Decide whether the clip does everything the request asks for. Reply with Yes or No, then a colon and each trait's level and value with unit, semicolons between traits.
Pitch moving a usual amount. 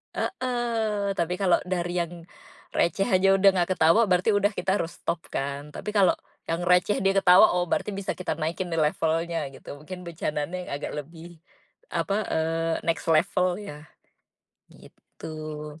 Yes: average, 3.1 semitones